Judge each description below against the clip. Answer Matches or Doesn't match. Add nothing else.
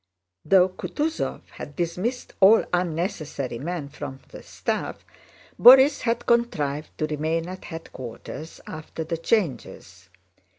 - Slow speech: Matches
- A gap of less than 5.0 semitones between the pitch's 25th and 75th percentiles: Doesn't match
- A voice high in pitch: Doesn't match